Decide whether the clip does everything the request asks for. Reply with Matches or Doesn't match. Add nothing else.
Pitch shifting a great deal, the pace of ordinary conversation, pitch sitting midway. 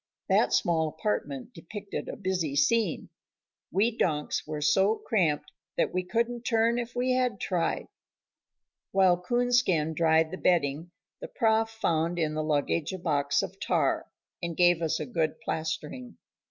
Matches